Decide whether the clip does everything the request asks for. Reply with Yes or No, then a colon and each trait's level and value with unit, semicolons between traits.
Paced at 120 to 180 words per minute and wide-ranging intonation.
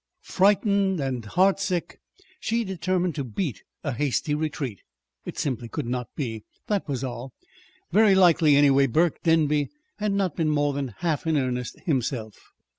Yes: average, 150 wpm; wide, 6.0 semitones